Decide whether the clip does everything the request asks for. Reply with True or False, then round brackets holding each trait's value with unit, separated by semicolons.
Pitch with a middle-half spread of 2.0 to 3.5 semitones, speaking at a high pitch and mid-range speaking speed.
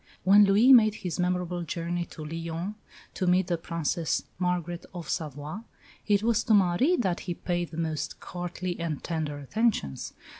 False (2.7 semitones; 175 Hz; 160 wpm)